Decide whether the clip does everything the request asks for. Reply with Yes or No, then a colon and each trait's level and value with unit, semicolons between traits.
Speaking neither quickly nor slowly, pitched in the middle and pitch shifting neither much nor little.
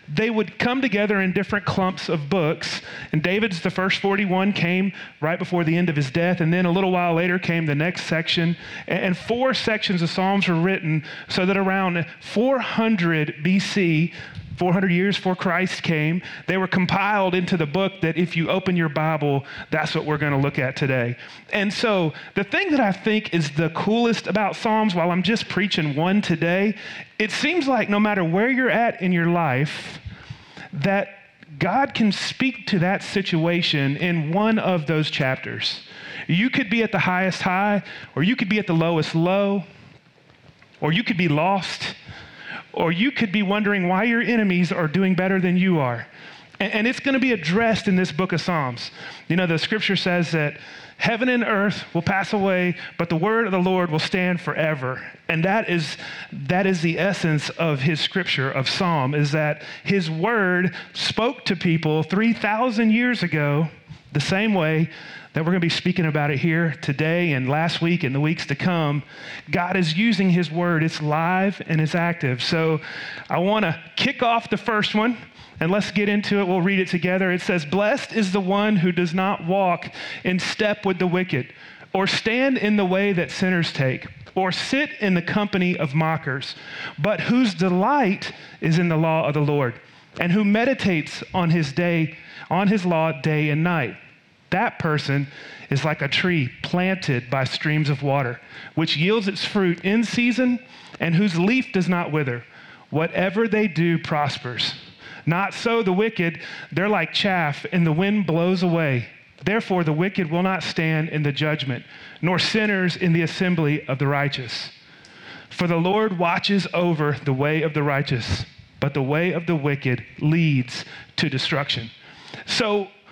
Yes: average, 185 wpm; medium, 175 Hz; average, 4.1 semitones